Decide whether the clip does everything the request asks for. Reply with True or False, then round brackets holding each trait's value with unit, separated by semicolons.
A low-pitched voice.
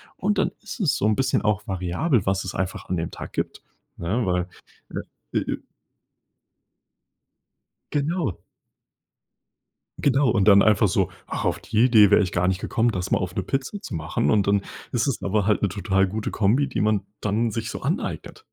True (105 Hz)